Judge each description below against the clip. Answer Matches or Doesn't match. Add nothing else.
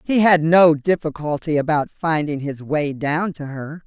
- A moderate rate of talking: Matches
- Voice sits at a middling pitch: Matches